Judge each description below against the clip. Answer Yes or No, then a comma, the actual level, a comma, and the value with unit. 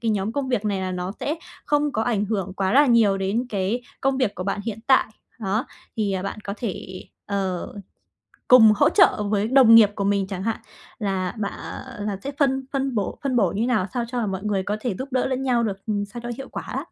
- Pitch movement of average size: Yes, average, 4.0 semitones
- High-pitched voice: Yes, high, 215 Hz